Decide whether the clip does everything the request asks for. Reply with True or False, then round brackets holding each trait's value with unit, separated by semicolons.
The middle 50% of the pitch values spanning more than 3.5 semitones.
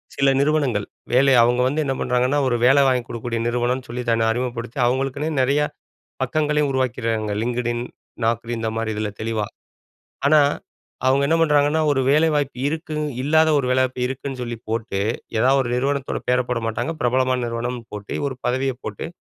False (2.8 semitones)